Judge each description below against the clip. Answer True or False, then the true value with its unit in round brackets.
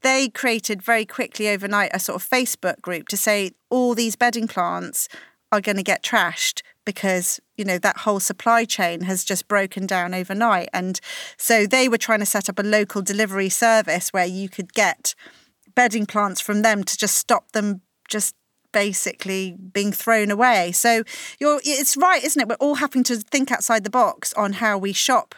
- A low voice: False (215 Hz)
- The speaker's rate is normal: True (190 wpm)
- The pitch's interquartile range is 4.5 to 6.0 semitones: False (3.6 semitones)